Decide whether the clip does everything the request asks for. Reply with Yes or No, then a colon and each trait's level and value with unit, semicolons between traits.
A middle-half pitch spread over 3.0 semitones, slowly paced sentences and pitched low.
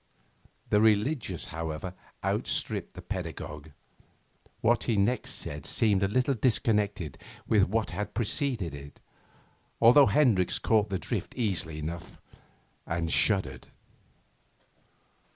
Yes: average, 5.1 semitones; slow, 110 wpm; low, 100 Hz